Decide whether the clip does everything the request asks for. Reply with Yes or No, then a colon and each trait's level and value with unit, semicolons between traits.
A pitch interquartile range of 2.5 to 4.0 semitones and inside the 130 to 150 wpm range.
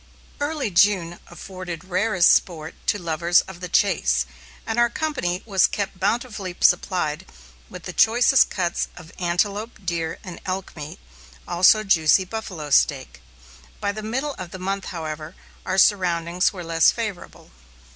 Yes: average, 3.4 semitones; average, 140 wpm